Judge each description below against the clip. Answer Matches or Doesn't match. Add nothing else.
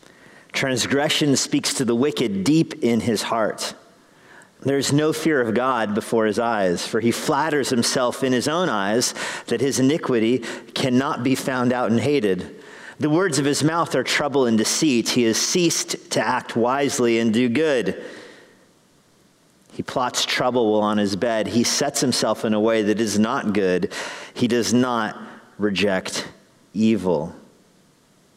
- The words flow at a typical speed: Matches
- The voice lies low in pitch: Matches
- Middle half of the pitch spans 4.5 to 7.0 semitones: Doesn't match